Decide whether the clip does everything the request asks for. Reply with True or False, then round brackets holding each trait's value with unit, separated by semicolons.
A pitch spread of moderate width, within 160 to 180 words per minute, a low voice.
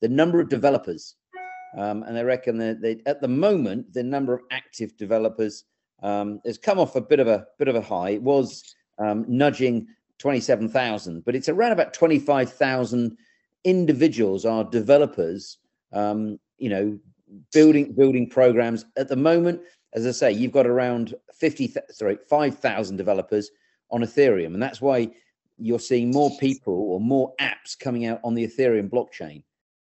True (4.3 semitones; 170 wpm; 125 Hz)